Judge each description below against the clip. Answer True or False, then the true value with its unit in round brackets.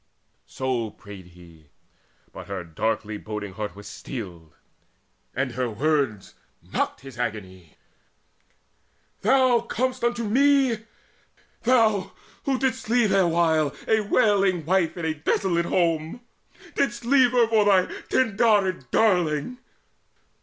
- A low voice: False (170 Hz)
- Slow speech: True (115 wpm)